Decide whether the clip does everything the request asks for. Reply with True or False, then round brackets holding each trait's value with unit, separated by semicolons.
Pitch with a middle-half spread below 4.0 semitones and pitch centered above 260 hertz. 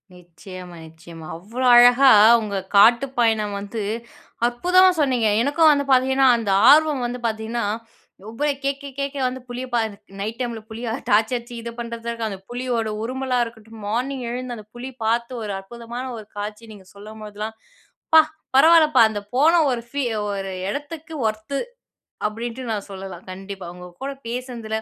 False (3.5 semitones; 235 Hz)